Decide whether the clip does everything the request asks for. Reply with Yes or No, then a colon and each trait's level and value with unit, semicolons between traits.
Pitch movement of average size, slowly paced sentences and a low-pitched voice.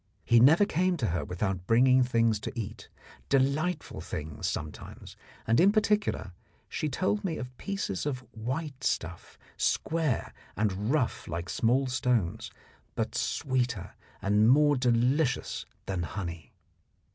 No: wide, 6.3 semitones; slow, 130 wpm; low, 125 Hz